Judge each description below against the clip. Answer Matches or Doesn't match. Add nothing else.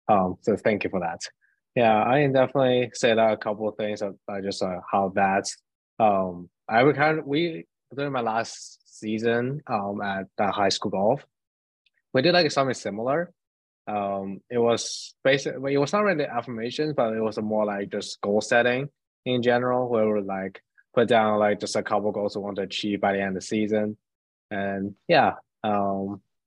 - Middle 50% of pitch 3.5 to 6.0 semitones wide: Matches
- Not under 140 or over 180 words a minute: Doesn't match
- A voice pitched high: Doesn't match